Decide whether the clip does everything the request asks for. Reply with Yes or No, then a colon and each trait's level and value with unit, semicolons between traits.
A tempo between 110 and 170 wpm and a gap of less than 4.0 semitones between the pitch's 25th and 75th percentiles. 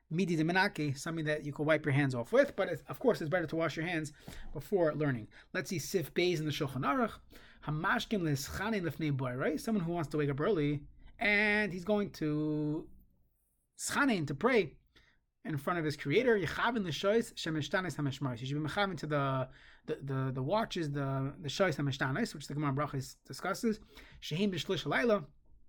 No: average, 165 wpm; average, 5.0 semitones